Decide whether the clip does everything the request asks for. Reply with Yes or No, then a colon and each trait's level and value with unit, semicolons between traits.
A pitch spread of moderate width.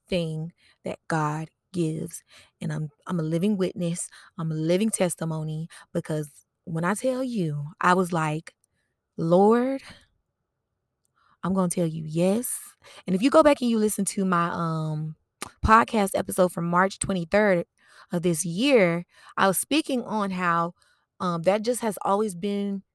Yes: average, 3.5 semitones